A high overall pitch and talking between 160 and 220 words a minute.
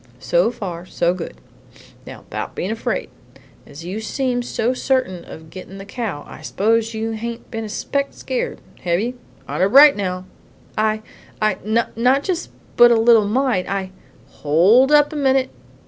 Yes: high, 220 Hz; average, 165 wpm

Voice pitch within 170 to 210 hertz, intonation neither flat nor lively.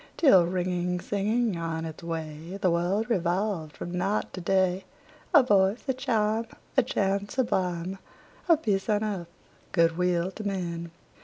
Yes: high, 190 Hz; average, 3.6 semitones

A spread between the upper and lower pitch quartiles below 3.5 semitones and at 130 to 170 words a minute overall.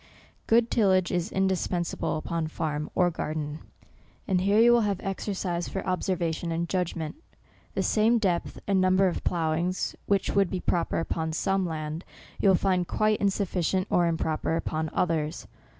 Yes: average, 2.9 semitones; average, 155 wpm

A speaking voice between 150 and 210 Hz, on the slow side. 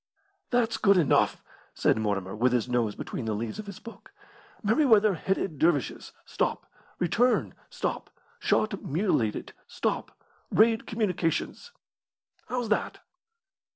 Yes: medium, 185 Hz; slow, 120 wpm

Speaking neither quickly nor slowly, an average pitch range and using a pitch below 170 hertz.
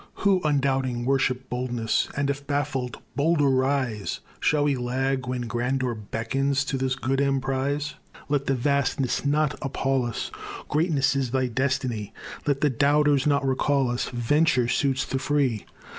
No: average, 145 wpm; narrow, 2.0 semitones; low, 135 Hz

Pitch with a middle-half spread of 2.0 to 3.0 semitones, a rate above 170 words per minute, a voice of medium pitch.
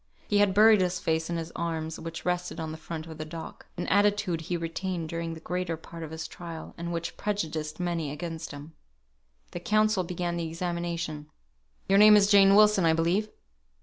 Yes: narrow, 2.5 semitones; average, 195 wpm; medium, 170 Hz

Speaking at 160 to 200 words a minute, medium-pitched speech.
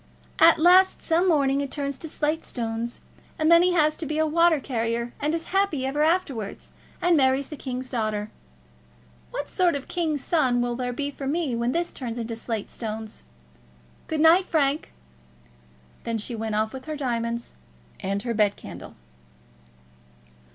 No: average, 170 wpm; very high, 275 Hz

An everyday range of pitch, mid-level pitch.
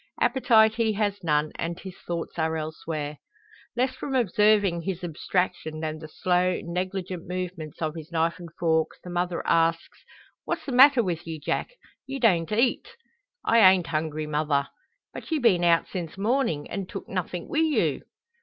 Yes: average, 4.5 semitones; medium, 175 Hz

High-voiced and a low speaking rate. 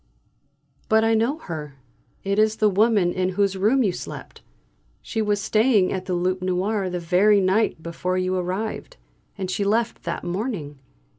No: high, 195 Hz; average, 165 wpm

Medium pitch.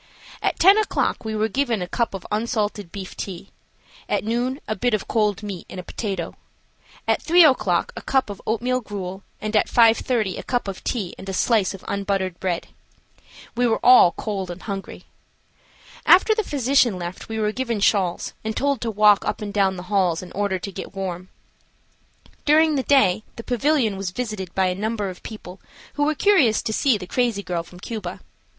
No: high, 210 Hz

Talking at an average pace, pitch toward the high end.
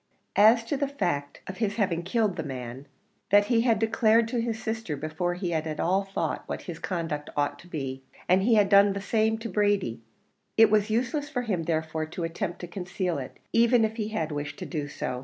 No: fast, 220 wpm; high, 195 Hz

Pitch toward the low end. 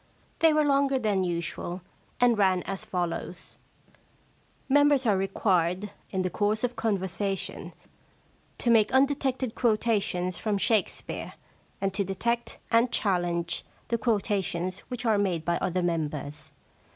No: high, 200 Hz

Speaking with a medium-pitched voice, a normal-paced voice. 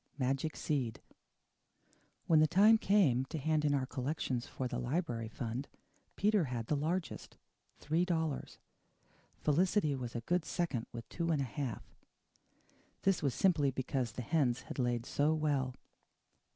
Yes: medium, 145 Hz; average, 150 wpm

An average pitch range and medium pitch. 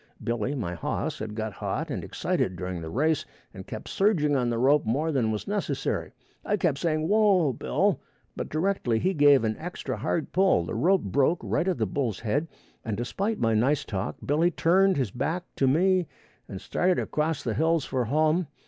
No: wide, 7.2 semitones; medium, 145 Hz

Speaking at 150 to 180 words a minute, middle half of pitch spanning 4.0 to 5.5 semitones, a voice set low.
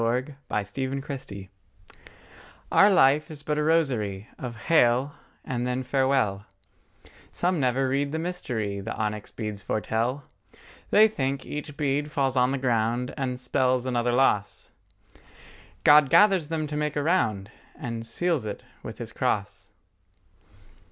No: average, 140 wpm; average, 4.3 semitones; low, 130 Hz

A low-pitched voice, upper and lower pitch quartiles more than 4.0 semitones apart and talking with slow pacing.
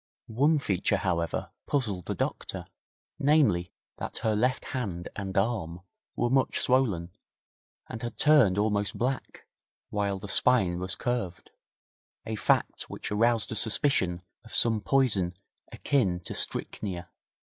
Yes: low, 105 Hz; average, 5.1 semitones; slow, 130 wpm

